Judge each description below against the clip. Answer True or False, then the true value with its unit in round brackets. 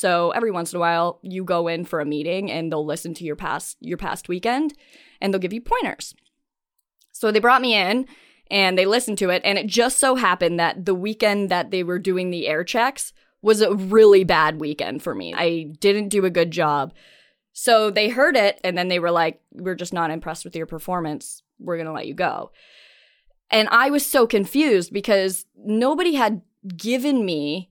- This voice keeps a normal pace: False (210 wpm)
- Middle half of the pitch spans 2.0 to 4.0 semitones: False (5.0 semitones)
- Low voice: False (190 Hz)